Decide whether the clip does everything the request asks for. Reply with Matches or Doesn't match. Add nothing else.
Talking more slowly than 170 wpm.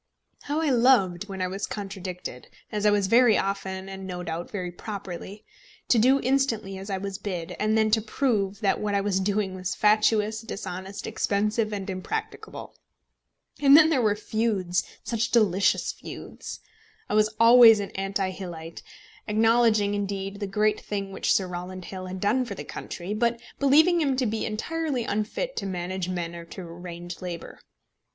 Doesn't match